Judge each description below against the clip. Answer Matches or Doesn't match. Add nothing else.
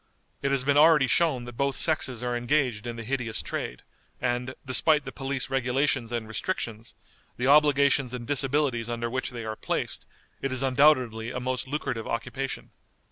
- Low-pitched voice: Matches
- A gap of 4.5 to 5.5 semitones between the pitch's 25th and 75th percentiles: Doesn't match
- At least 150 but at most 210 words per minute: Matches